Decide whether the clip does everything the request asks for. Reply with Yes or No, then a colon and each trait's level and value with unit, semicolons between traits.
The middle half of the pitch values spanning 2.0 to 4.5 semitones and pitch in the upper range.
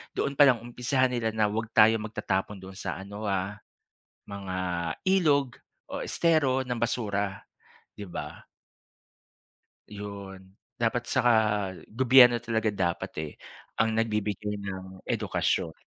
No: average, 3.6 semitones; low, 110 Hz